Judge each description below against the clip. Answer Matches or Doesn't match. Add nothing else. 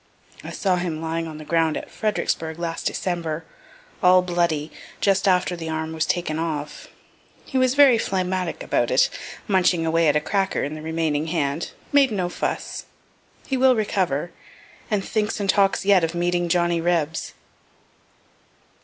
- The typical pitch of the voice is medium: Matches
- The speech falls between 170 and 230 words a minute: Doesn't match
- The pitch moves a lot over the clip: Doesn't match